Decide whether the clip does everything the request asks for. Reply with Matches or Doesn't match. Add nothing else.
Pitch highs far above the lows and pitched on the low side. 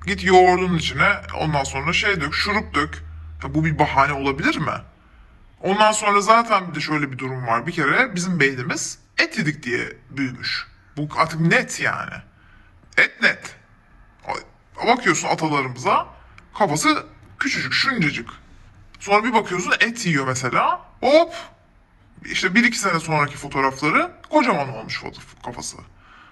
Doesn't match